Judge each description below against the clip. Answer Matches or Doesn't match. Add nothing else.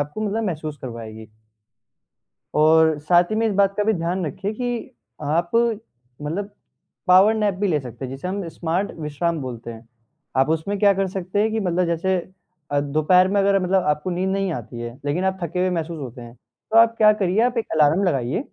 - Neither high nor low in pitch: Matches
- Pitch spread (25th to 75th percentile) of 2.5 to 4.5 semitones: Doesn't match